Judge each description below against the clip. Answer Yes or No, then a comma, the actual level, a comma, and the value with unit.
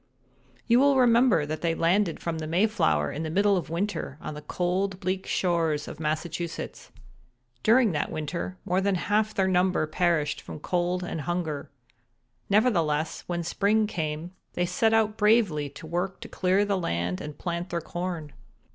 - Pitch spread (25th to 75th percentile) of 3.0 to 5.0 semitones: Yes, average, 4.2 semitones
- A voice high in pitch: No, medium, 175 Hz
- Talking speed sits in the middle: Yes, average, 165 wpm